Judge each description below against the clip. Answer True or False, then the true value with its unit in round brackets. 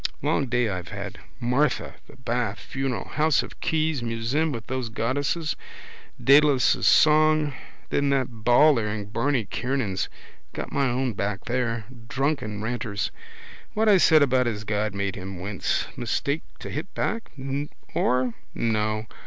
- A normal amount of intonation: True (4.6 semitones)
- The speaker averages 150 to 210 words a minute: False (140 wpm)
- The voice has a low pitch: True (125 Hz)